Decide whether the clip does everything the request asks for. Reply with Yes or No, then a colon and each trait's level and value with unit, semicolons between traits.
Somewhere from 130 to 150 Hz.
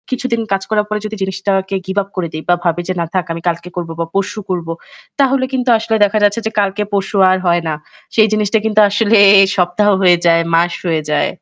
No: high, 195 Hz